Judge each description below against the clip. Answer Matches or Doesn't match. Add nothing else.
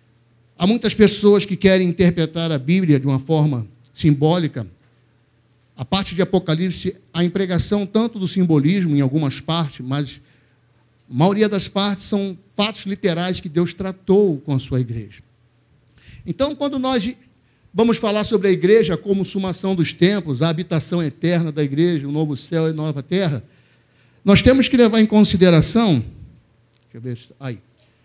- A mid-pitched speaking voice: Matches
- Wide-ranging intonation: Matches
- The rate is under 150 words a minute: Doesn't match